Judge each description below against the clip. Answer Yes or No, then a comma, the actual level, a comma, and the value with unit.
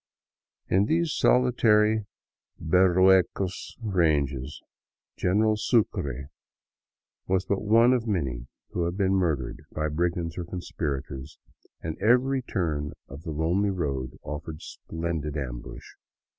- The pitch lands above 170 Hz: No, very low, 85 Hz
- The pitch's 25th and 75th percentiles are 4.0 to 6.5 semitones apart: Yes, wide, 5.5 semitones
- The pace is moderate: No, slow, 110 wpm